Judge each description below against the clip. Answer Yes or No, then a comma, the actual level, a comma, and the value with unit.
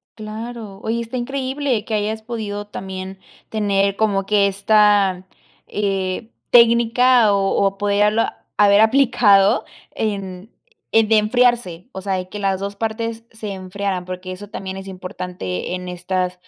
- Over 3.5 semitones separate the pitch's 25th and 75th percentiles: No, average, 2.7 semitones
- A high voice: Yes, high, 205 Hz